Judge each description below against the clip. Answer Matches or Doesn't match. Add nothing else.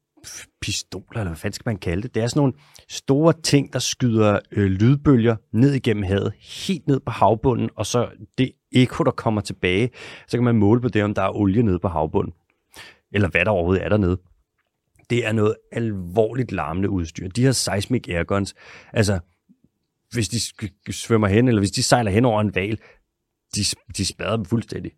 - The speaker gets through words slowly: Doesn't match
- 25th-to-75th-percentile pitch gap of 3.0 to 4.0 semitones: Matches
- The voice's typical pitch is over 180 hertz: Doesn't match